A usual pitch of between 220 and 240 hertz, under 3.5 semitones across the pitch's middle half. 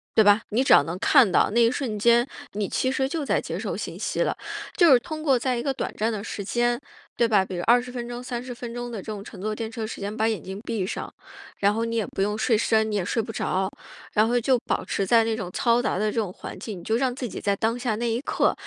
Yes: high, 225 Hz; average, 2.7 semitones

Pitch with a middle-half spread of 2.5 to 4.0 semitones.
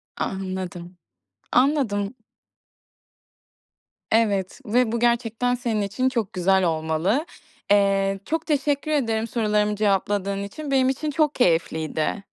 No: average, 4.5 semitones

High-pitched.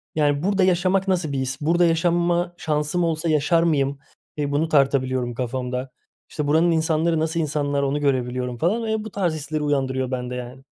No: medium, 150 Hz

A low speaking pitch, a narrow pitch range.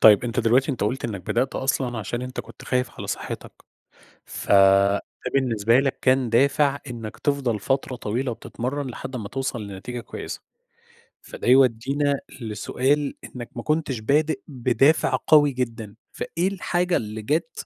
No: low, 125 Hz; average, 3.4 semitones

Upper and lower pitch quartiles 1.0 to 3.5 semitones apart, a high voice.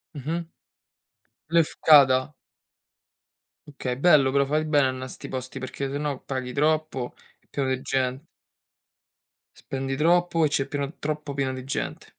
No: narrow, 2.6 semitones; medium, 140 Hz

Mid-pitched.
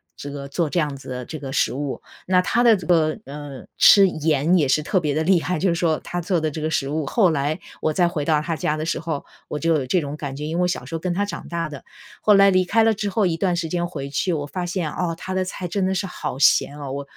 Yes: medium, 165 Hz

